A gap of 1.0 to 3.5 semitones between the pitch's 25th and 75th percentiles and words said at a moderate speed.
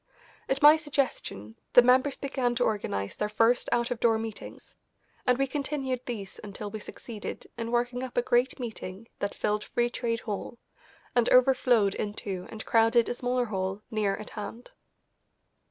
Yes: average, 3.1 semitones; average, 165 wpm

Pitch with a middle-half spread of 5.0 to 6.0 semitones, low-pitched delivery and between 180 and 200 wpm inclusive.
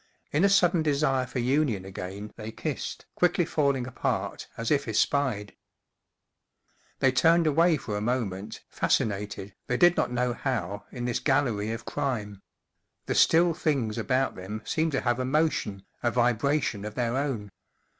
No: average, 5.3 semitones; low, 125 Hz; average, 165 wpm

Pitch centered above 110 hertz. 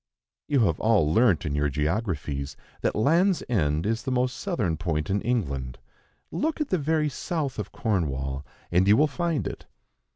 No: low, 105 Hz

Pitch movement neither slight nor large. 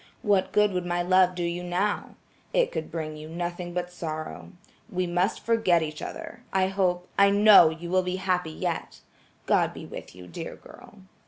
No: narrow, 1.9 semitones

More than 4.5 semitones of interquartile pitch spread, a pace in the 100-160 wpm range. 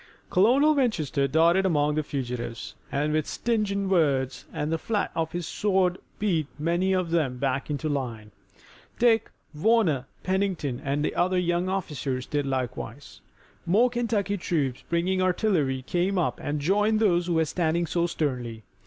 Yes: average, 5.2 semitones; average, 150 wpm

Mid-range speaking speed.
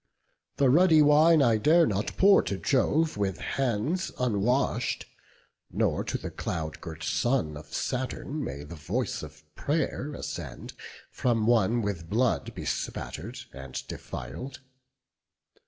No: slow, 125 wpm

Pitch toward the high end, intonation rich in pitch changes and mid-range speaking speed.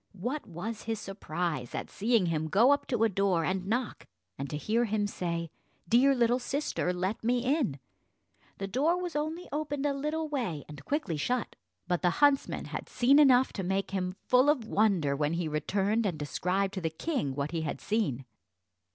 Yes: high, 205 Hz; wide, 7.1 semitones; average, 190 wpm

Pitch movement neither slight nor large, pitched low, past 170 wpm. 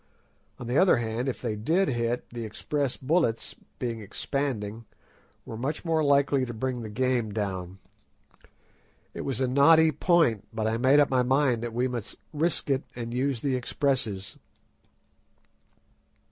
No: average, 3.8 semitones; low, 125 Hz; average, 155 wpm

